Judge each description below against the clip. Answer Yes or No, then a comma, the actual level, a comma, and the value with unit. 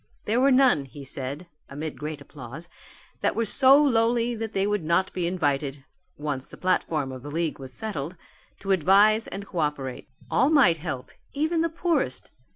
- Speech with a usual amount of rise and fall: No, wide, 8.0 semitones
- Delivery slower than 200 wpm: Yes, average, 175 wpm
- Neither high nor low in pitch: Yes, medium, 175 Hz